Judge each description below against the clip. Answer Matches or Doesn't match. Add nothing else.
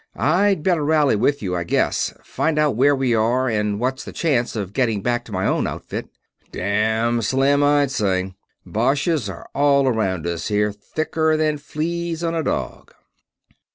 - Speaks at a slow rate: Doesn't match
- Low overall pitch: Matches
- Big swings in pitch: Matches